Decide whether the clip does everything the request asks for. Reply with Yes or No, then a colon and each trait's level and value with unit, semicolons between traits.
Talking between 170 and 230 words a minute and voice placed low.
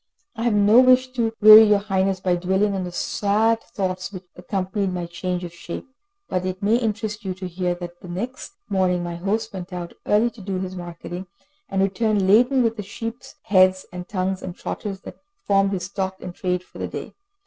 No: fast, 205 wpm; high, 190 Hz